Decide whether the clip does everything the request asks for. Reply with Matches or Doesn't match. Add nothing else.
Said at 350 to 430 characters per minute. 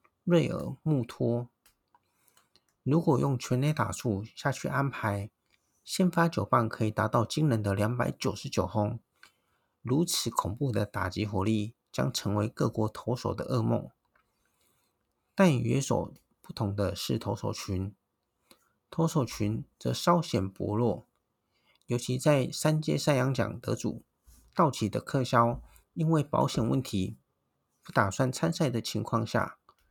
Doesn't match